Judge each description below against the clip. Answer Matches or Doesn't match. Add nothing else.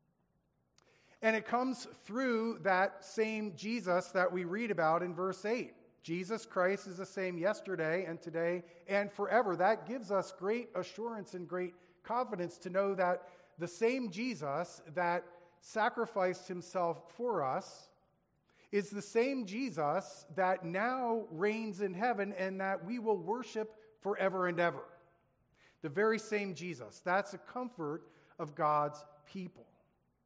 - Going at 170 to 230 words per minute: Doesn't match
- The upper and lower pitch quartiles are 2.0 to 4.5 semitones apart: Matches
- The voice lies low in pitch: Doesn't match